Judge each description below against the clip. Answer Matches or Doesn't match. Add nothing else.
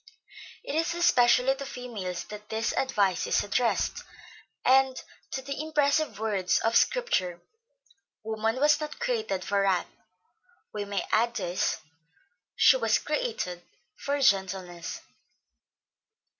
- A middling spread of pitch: Doesn't match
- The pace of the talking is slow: Matches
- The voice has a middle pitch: Doesn't match